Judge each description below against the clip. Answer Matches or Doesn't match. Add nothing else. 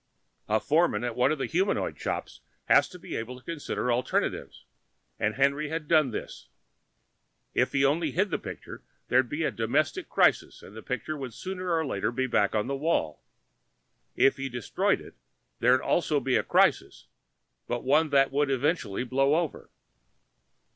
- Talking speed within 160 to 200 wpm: Matches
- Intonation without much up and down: Doesn't match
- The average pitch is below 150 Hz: Matches